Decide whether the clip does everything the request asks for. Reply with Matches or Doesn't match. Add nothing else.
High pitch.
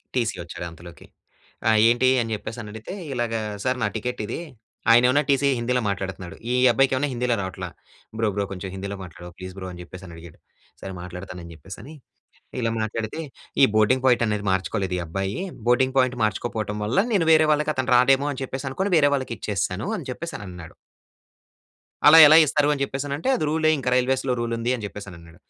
Doesn't match